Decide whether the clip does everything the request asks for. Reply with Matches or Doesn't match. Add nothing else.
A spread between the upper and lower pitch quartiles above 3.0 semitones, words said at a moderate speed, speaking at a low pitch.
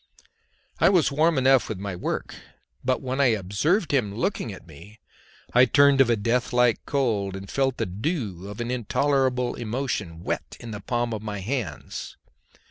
Matches